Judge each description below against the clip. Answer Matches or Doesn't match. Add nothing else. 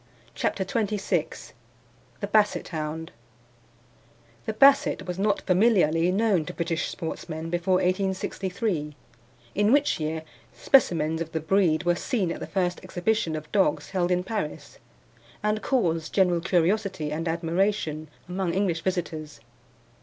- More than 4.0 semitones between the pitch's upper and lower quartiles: Doesn't match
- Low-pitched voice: Doesn't match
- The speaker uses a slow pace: Matches